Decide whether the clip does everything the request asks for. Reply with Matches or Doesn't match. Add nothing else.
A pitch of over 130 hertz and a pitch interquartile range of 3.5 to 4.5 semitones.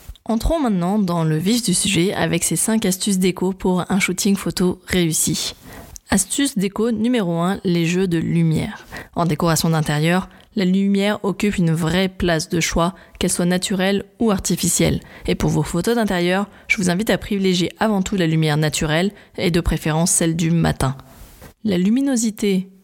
Doesn't match